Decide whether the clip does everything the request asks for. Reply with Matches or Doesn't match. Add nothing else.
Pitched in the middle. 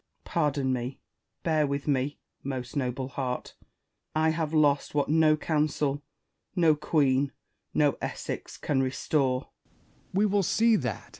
Matches